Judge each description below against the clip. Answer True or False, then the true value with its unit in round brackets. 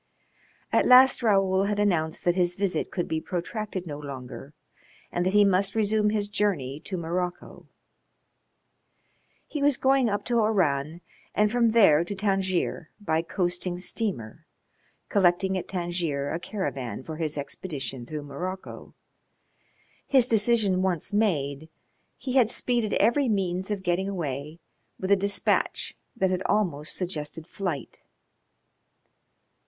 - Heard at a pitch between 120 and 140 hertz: False (185 Hz)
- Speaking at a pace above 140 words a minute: False (135 wpm)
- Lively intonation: False (4.6 semitones)